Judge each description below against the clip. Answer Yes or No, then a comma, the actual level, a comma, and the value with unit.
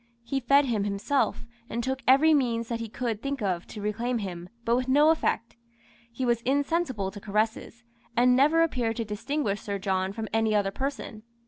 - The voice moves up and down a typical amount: Yes, average, 4.2 semitones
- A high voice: Yes, high, 235 Hz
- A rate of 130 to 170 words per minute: No, average, 190 wpm